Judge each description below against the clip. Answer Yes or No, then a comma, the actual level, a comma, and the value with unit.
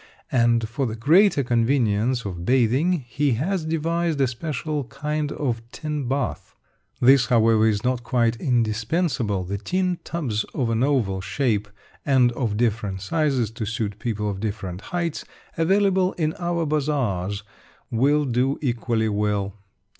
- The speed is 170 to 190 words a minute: No, average, 140 wpm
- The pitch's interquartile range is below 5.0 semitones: No, wide, 5.4 semitones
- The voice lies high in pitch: No, low, 125 Hz